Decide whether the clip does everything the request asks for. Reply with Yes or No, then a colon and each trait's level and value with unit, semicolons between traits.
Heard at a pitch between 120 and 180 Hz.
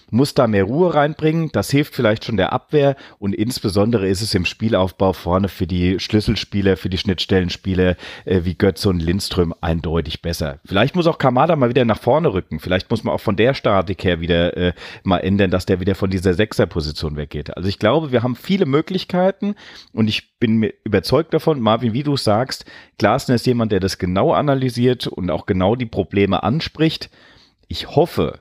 No: low, 100 Hz